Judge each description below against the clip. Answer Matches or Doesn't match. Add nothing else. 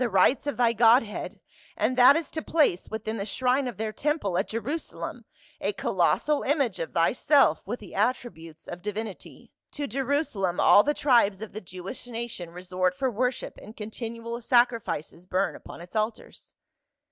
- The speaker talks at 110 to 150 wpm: Doesn't match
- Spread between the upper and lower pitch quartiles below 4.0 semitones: Doesn't match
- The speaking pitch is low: Doesn't match